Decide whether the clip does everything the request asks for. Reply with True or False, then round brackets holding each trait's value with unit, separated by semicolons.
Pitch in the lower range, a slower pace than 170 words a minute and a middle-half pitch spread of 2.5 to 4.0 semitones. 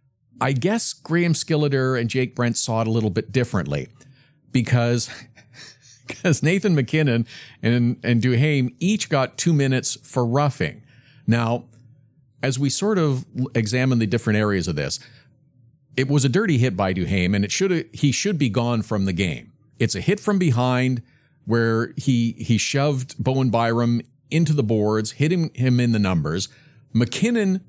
True (130 Hz; 160 wpm; 3.7 semitones)